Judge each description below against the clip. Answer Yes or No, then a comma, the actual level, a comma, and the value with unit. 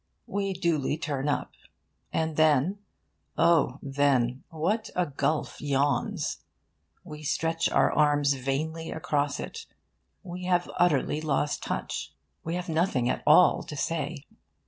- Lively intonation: No, average, 3.2 semitones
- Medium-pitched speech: Yes, medium, 155 Hz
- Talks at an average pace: No, slow, 125 wpm